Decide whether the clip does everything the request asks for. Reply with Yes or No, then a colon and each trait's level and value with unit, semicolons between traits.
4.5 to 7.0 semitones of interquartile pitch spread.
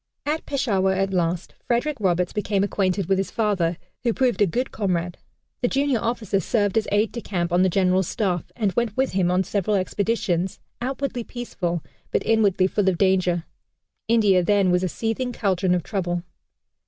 No: average, 3.7 semitones